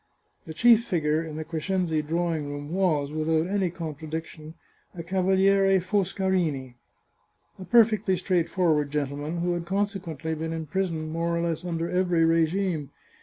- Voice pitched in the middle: Yes, medium, 170 Hz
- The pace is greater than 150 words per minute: No, average, 140 wpm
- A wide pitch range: No, average, 3.2 semitones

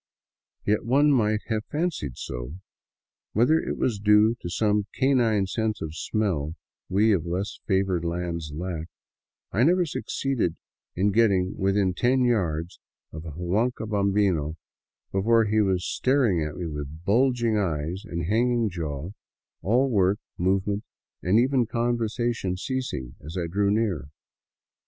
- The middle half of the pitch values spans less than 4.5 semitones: No, average, 5.1 semitones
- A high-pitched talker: No, low, 100 Hz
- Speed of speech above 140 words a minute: No, slow, 135 wpm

